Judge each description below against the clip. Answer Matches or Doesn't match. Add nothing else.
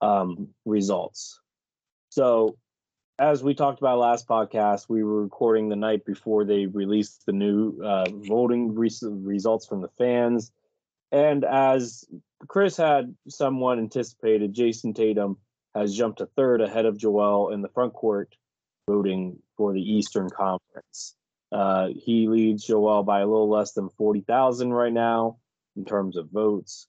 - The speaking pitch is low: Matches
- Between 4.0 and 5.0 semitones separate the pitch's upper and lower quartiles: Doesn't match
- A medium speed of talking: Matches